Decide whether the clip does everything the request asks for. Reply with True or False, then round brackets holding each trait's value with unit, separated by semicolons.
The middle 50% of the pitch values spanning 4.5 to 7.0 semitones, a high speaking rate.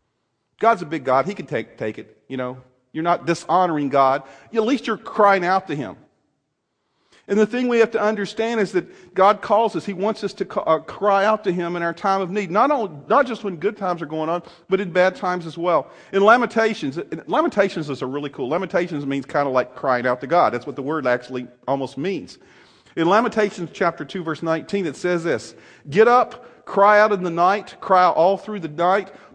True (5.1 semitones; 225 wpm)